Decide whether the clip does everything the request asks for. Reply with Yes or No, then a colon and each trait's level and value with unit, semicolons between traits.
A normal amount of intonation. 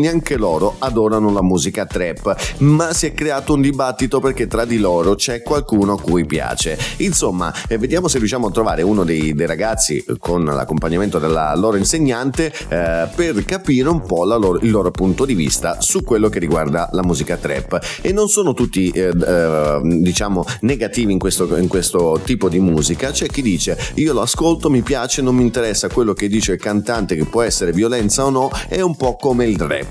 No: wide, 7.3 semitones